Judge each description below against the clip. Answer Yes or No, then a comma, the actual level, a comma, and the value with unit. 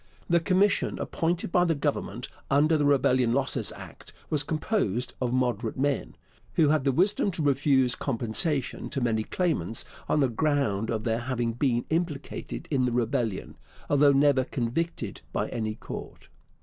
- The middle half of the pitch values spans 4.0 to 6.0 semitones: Yes, average, 4.5 semitones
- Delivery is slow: No, average, 155 wpm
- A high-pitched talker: No, low, 135 Hz